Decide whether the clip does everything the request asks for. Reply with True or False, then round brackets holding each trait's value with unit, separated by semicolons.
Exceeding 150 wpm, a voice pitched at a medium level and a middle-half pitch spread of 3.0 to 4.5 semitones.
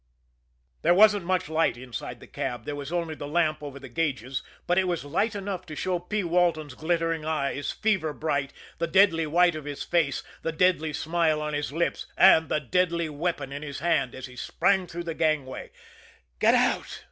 True (195 wpm; 160 Hz; 3.3 semitones)